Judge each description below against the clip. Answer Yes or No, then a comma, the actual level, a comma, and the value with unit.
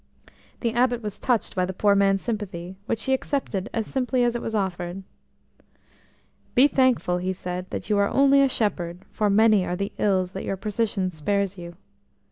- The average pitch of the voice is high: Yes, high, 200 Hz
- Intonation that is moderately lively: Yes, average, 4.1 semitones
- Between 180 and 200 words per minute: Yes, average, 185 wpm